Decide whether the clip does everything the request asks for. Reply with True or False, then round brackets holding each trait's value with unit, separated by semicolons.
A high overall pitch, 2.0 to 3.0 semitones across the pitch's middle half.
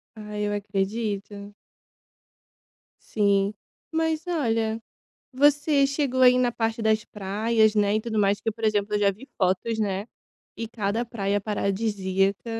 True (215 Hz; 2.5 semitones)